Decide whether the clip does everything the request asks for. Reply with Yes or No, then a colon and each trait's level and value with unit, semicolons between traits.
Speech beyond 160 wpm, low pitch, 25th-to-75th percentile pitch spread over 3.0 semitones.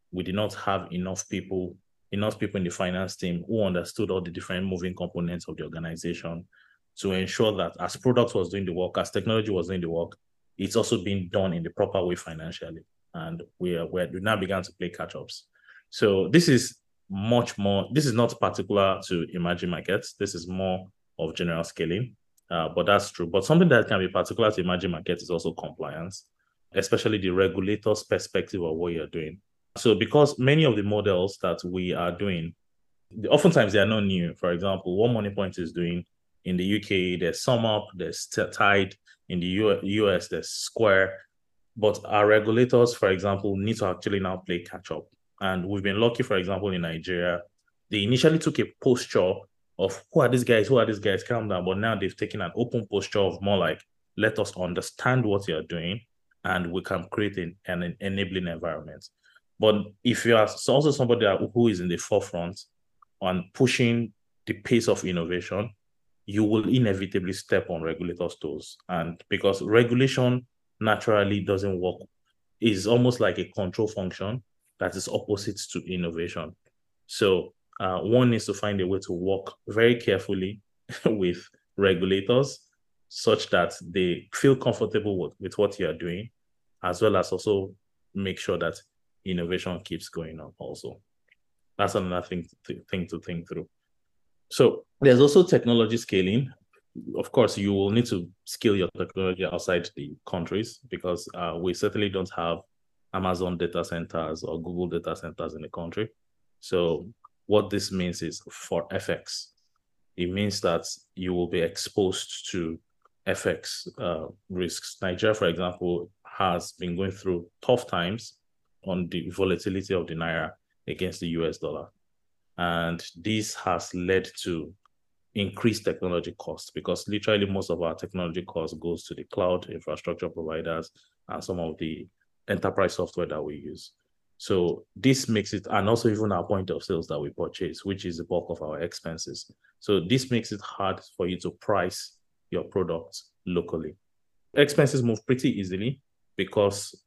Yes: average, 170 wpm; very low, 95 Hz; average, 3.4 semitones